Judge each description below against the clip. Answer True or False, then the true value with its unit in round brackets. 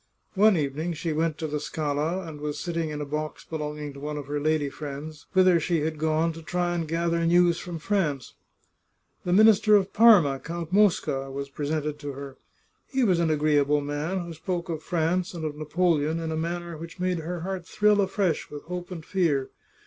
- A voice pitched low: False (160 Hz)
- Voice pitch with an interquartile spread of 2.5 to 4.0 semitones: True (2.9 semitones)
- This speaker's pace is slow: False (200 wpm)